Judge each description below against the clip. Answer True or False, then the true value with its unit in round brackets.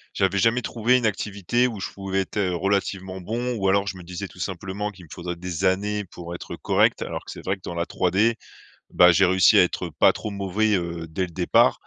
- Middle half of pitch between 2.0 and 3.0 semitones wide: True (2.6 semitones)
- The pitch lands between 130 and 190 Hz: False (95 Hz)